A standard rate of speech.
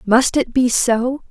Yes: average, 185 wpm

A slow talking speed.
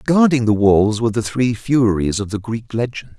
No: fast, 205 wpm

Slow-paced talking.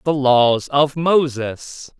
Yes: slow, 120 wpm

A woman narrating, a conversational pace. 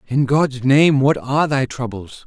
No: male; average, 185 wpm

